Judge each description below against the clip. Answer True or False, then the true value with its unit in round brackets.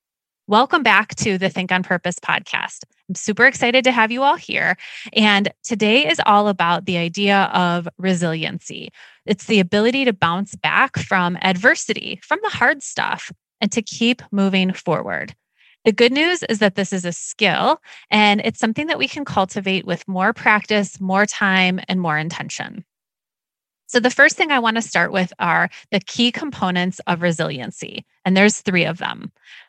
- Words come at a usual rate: True (175 wpm)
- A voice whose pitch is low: False (205 Hz)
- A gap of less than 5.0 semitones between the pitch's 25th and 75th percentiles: True (4.2 semitones)